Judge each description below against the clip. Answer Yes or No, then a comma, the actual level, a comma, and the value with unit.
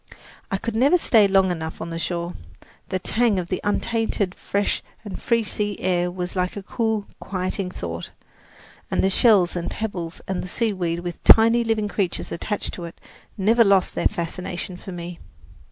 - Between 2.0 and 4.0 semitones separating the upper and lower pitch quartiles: Yes, average, 3.4 semitones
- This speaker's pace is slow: No, average, 175 wpm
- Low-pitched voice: No, high, 190 Hz